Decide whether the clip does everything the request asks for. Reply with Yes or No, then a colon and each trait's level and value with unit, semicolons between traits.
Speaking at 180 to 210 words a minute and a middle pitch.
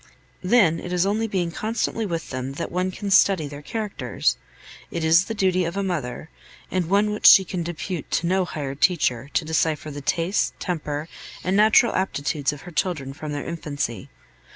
Yes: average, 190 wpm; medium, 170 Hz